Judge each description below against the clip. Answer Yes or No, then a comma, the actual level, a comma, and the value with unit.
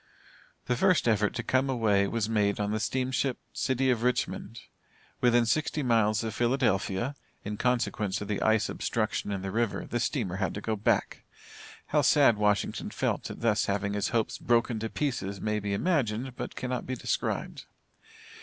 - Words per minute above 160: Yes, average, 175 wpm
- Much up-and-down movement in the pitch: No, average, 3.4 semitones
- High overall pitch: No, low, 115 Hz